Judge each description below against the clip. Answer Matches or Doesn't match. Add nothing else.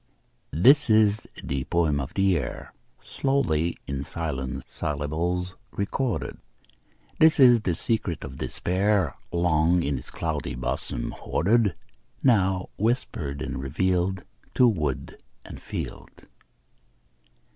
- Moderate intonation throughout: Doesn't match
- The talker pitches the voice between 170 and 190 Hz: Doesn't match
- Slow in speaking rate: Matches